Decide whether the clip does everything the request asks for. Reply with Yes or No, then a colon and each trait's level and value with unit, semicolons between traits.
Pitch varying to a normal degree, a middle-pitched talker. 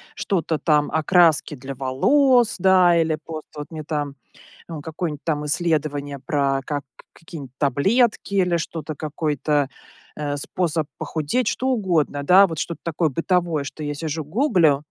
Yes: average, 3.3 semitones; medium, 155 Hz